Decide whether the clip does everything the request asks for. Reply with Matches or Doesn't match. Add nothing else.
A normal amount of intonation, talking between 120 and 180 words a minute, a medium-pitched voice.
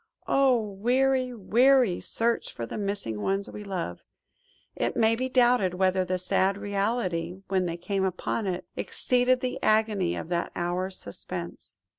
Doesn't match